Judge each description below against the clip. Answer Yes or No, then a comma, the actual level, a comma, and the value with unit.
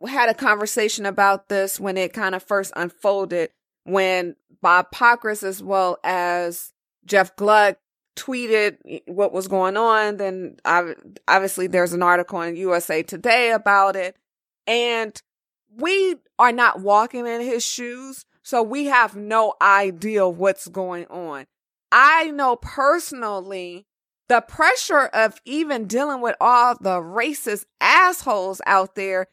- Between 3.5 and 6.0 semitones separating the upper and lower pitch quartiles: Yes, average, 4.2 semitones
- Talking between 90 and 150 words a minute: Yes, slow, 135 wpm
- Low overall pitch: No, high, 205 Hz